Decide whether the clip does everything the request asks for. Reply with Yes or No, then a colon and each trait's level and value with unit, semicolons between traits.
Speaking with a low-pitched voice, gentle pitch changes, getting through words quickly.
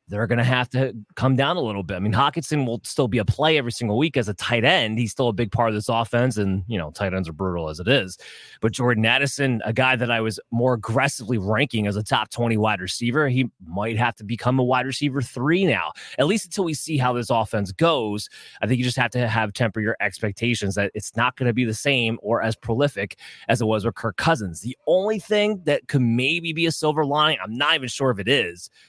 No: low, 120 Hz; average, 3.8 semitones; fast, 255 wpm